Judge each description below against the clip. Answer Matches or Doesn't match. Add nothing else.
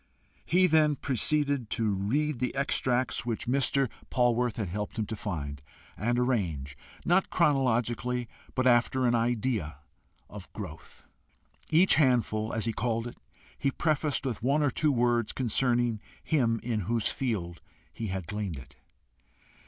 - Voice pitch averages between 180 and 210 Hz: Doesn't match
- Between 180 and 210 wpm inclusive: Doesn't match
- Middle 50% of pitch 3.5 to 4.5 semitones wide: Matches